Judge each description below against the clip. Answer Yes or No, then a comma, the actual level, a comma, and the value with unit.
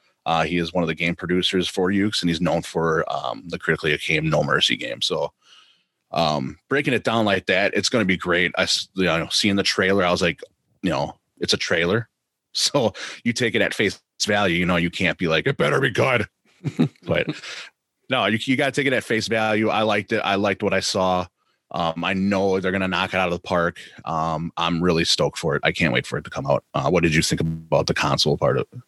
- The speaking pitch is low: Yes, very low, 95 Hz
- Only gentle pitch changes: No, average, 3.0 semitones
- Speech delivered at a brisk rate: Yes, fast, 250 wpm